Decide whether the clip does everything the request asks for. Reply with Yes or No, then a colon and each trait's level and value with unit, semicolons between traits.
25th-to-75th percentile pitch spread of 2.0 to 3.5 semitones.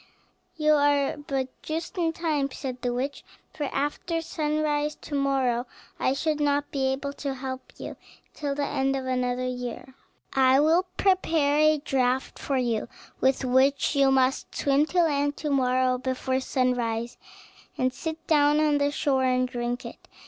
Yes: narrow, 2.5 semitones